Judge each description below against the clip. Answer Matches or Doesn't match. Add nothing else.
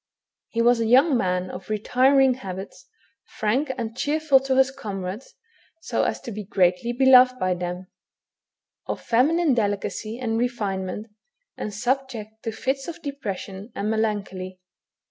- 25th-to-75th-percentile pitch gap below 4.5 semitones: Doesn't match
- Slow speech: Doesn't match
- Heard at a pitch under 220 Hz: Doesn't match